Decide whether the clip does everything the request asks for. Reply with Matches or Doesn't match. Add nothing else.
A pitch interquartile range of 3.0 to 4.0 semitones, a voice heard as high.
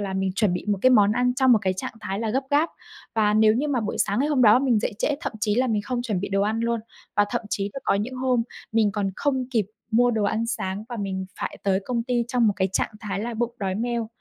Matches